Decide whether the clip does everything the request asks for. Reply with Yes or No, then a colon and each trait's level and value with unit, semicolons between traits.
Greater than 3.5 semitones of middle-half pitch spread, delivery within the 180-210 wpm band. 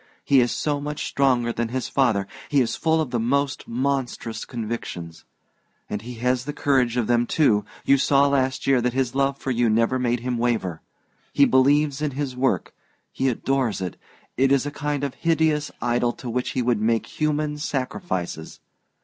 No: average, 3.0 semitones; average, 185 wpm